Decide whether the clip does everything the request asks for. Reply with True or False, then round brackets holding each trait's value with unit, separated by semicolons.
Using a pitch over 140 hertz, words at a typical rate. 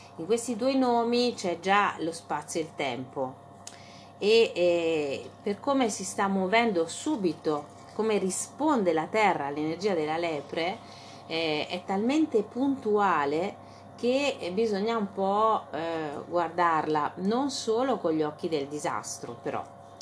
True (185 Hz; 130 wpm)